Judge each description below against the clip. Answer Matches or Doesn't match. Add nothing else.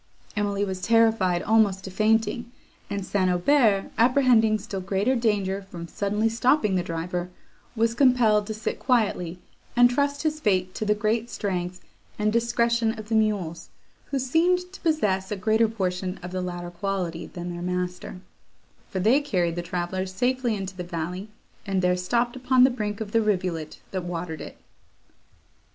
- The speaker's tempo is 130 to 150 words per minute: Doesn't match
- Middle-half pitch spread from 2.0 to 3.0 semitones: Doesn't match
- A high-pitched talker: Matches